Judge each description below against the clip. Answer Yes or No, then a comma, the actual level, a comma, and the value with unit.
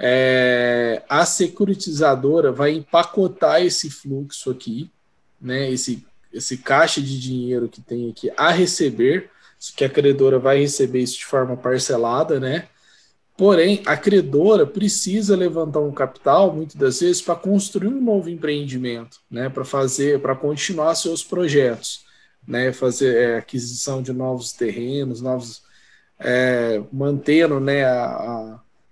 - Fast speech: No, average, 135 wpm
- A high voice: No, low, 135 Hz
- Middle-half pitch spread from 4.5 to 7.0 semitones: Yes, average, 4.9 semitones